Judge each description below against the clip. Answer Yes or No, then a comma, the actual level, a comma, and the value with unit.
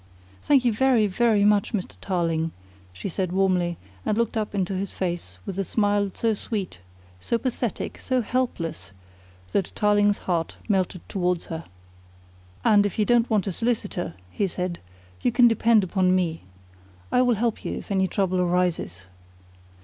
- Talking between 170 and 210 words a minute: No, average, 160 wpm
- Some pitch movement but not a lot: Yes, average, 3.6 semitones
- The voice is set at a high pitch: Yes, high, 195 Hz